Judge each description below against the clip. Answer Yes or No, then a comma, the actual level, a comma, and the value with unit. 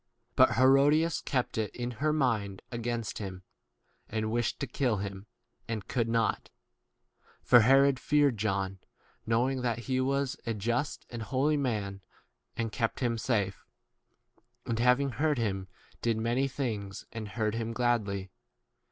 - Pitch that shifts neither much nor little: Yes, average, 3.4 semitones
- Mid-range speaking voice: No, low, 115 Hz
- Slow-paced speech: No, average, 150 wpm